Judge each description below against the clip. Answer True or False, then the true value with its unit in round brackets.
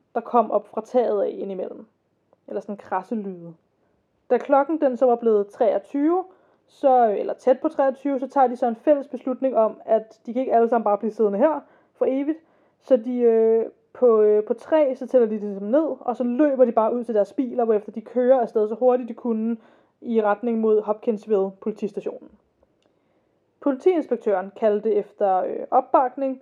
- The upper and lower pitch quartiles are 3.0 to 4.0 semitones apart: True (3.7 semitones)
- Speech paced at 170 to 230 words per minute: True (185 wpm)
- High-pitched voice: True (240 Hz)